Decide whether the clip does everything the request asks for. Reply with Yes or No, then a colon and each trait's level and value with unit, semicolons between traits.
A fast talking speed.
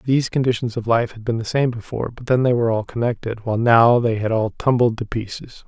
Yes: fast, 245 wpm